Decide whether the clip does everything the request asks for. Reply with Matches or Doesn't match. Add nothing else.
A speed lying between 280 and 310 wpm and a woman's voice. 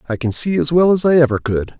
Doesn't match